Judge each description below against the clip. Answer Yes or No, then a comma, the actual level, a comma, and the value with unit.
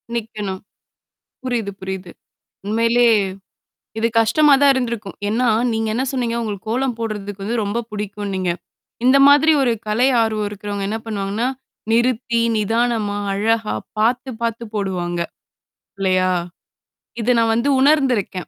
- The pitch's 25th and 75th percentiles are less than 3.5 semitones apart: Yes, average, 2.8 semitones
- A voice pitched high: Yes, high, 225 Hz